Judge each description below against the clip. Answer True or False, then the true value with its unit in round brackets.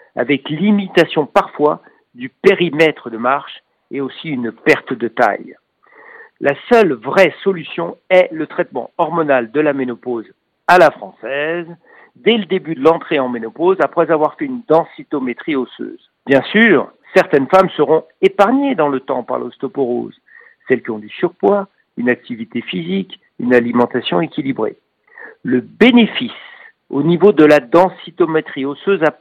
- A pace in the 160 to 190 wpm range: False (145 wpm)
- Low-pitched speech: False (165 Hz)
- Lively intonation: True (6.0 semitones)